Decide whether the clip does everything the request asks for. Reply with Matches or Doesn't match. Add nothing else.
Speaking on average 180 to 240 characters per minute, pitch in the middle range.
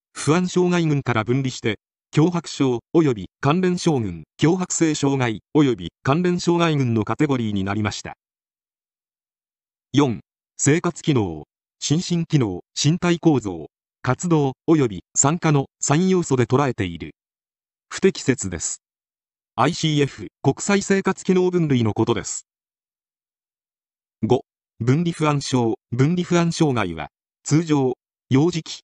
Matches